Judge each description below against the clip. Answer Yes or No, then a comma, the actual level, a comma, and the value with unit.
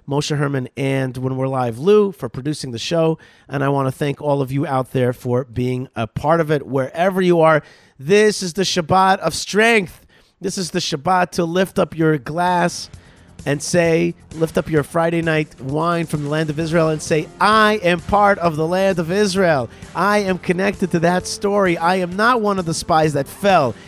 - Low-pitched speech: No, medium, 165 Hz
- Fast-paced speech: Yes, fast, 210 wpm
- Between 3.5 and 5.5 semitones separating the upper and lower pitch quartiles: Yes, average, 4.8 semitones